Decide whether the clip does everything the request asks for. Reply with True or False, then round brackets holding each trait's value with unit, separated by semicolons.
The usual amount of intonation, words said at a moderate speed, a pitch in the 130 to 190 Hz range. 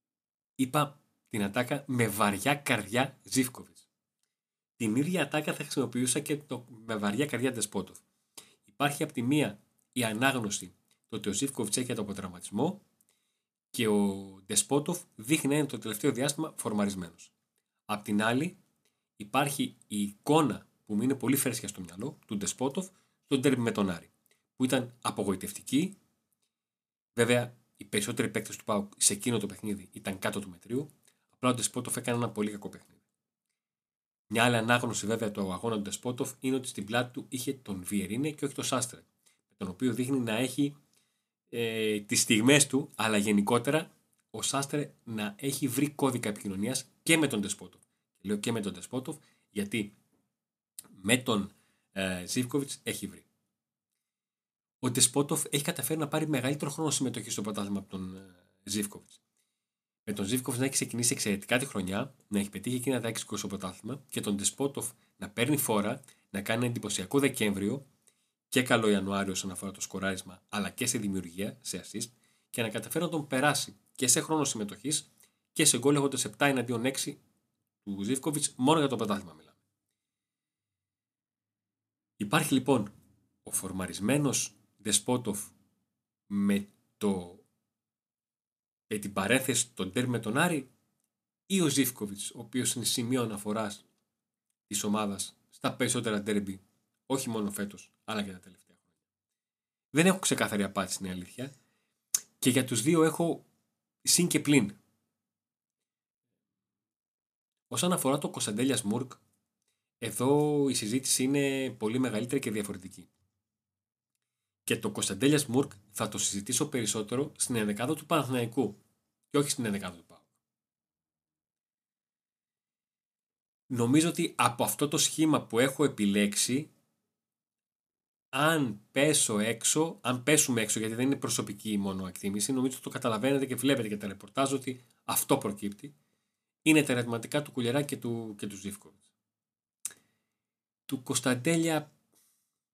False (5.0 semitones; 145 wpm; 120 Hz)